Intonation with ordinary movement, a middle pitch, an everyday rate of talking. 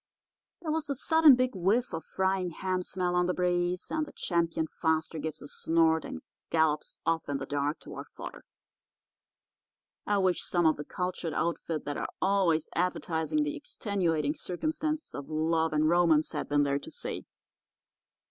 Yes: average, 3.3 semitones; medium, 170 Hz; average, 165 wpm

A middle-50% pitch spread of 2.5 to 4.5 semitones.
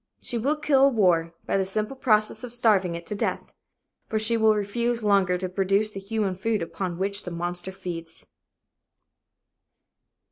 Yes: average, 3.5 semitones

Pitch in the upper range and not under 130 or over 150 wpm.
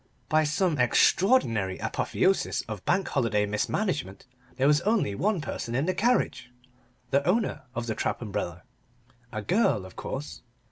No: low, 135 Hz; average, 145 wpm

